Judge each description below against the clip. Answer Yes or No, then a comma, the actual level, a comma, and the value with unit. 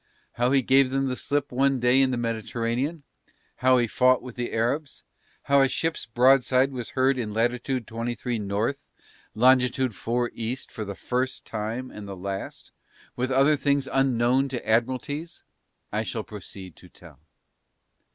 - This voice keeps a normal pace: Yes, average, 160 wpm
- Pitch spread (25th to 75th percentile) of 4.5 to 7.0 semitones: No, average, 2.7 semitones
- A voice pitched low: Yes, low, 125 Hz